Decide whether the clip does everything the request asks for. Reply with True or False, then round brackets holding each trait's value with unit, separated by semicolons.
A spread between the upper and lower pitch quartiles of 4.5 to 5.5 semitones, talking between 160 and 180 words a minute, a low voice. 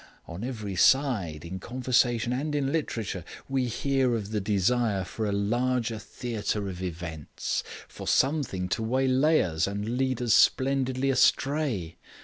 False (5.0 semitones; 140 wpm; 120 Hz)